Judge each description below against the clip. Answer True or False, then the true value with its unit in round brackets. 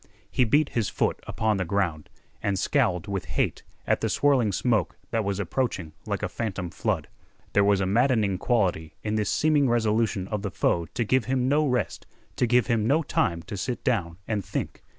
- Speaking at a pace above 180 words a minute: True (195 wpm)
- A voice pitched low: True (105 Hz)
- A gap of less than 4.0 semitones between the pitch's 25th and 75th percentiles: False (4.4 semitones)